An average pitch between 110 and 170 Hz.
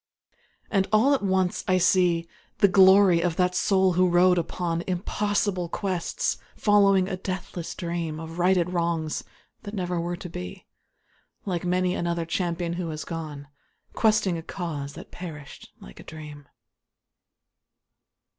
No: medium, 180 Hz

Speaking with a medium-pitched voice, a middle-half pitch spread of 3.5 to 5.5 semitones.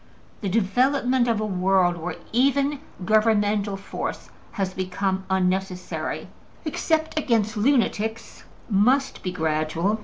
No: high, 205 Hz; average, 4.5 semitones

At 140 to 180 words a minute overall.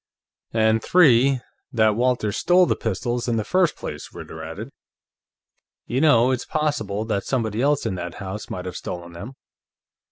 Yes: average, 160 wpm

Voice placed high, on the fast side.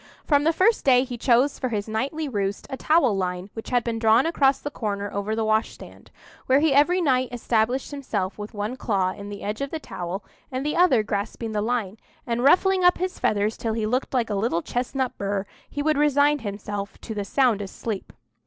Yes: high, 235 Hz; fast, 215 wpm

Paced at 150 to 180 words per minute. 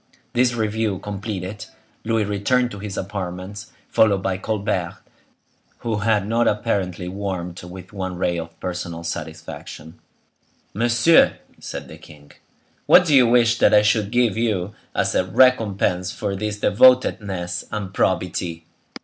No: slow, 135 wpm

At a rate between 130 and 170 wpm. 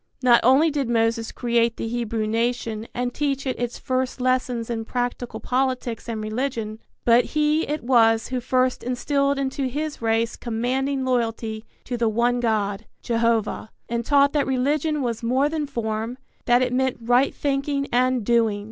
Yes: average, 165 wpm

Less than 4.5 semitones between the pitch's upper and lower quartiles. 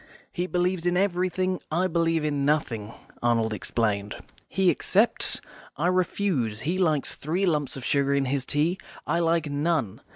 No: average, 4.8 semitones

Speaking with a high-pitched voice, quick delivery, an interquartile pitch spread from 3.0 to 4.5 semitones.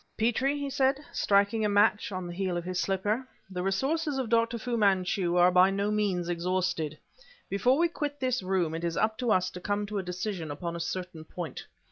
Yes: high, 195 Hz; fast, 210 wpm; average, 4.2 semitones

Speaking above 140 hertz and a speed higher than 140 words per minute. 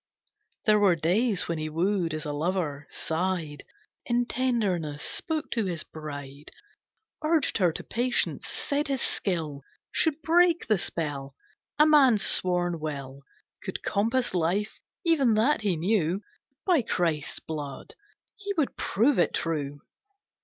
No: medium, 185 Hz; slow, 135 wpm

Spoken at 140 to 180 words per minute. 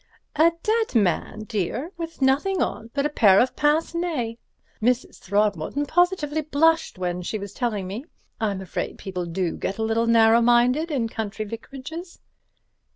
Yes: average, 160 wpm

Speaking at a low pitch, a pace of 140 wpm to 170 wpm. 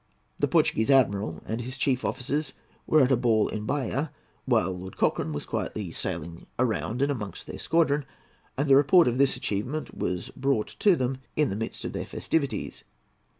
No: low, 125 Hz; average, 180 wpm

